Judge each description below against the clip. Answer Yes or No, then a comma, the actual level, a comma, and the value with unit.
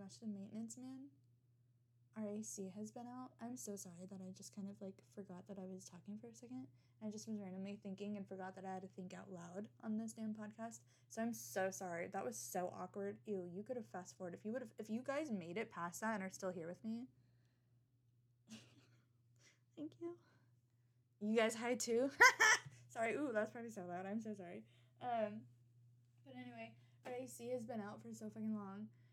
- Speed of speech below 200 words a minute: No, fast, 205 wpm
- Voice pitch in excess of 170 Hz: Yes, high, 190 Hz